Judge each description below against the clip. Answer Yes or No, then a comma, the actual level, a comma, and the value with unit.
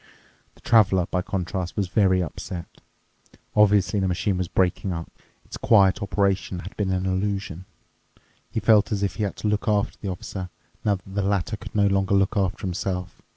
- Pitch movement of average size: No, narrow, 1.8 semitones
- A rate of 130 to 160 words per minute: No, average, 185 wpm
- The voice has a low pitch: Yes, very low, 95 Hz